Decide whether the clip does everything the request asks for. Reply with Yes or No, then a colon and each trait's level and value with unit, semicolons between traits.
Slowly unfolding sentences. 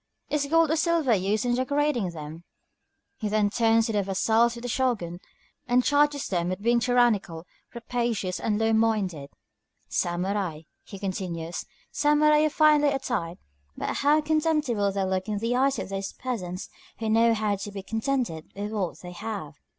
No: average, 165 wpm